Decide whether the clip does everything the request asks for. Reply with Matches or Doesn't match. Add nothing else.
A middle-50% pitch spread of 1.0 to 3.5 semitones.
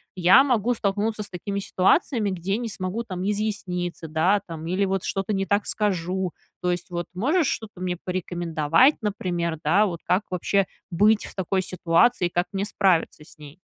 Matches